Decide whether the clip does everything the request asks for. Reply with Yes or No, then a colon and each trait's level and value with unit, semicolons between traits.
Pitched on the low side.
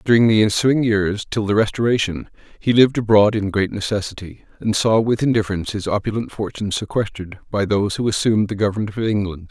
Yes: low, 105 Hz